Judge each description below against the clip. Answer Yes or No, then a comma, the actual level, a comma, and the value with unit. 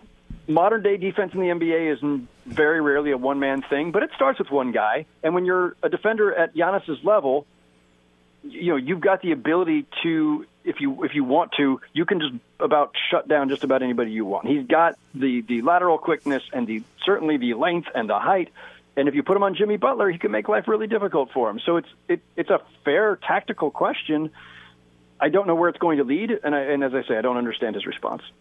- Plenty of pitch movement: Yes, wide, 6.3 semitones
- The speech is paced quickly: Yes, fast, 230 wpm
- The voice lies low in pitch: No, medium, 155 Hz